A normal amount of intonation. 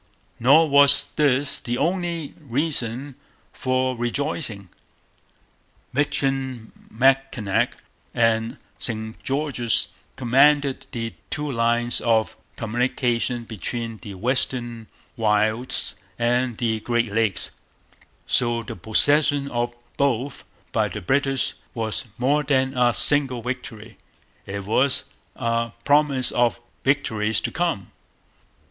Yes: average, 3.3 semitones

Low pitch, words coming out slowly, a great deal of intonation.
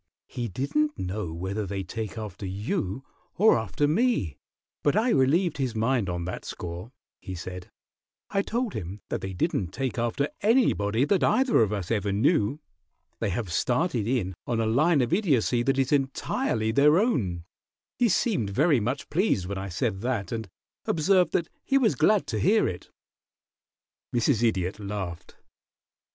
No: low, 115 Hz; average, 165 wpm; wide, 7.5 semitones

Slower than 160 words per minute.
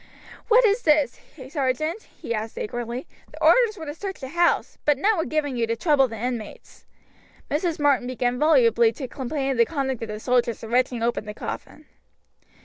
No: average, 190 wpm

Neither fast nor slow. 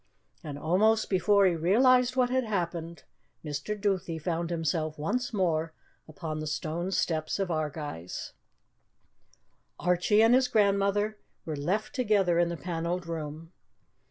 No: slow, 130 wpm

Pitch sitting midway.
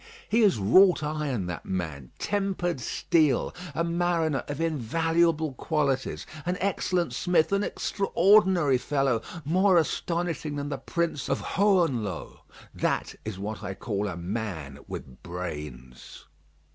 Yes: medium, 150 Hz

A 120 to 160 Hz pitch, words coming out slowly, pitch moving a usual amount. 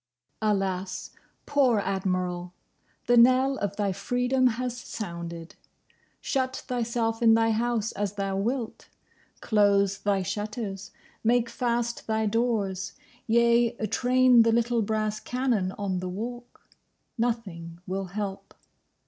No: high, 220 Hz; slow, 115 wpm; average, 3.6 semitones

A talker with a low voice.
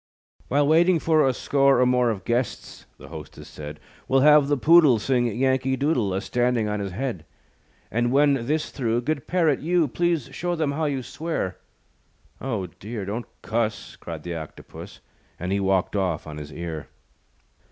Yes: low, 125 Hz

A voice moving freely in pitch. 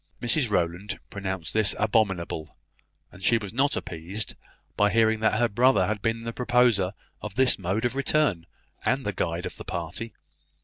No: average, 3.9 semitones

